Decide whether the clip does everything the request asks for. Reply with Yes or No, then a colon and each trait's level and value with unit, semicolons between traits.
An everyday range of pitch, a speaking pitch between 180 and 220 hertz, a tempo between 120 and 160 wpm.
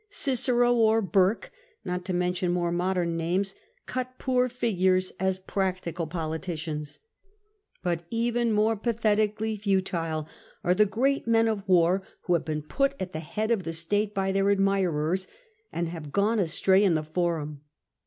Yes: average, 4.2 semitones; high, 190 Hz; average, 155 wpm